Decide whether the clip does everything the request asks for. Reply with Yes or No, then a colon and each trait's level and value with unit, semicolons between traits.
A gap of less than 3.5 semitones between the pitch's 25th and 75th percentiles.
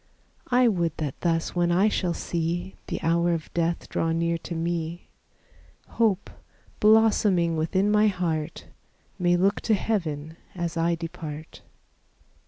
Yes: narrow, 2.6 semitones